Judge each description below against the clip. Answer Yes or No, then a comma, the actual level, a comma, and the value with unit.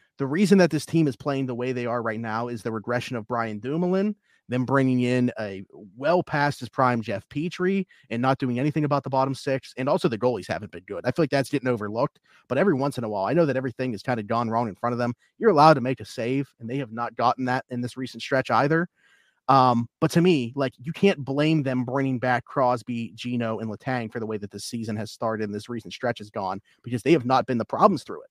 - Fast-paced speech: Yes, fast, 265 wpm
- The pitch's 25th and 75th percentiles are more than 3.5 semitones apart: No, average, 3.2 semitones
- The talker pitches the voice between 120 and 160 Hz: Yes, low, 125 Hz